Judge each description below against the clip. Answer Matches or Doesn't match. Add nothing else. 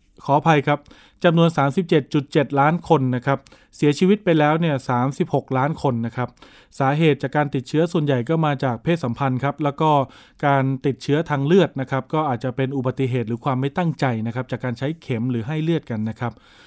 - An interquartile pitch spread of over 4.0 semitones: Doesn't match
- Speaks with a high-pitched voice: Doesn't match